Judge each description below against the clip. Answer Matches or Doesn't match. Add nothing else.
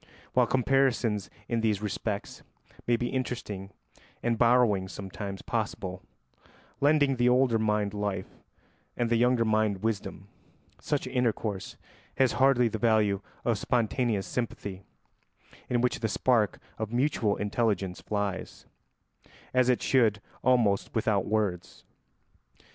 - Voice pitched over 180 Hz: Doesn't match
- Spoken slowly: Matches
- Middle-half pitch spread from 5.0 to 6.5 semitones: Doesn't match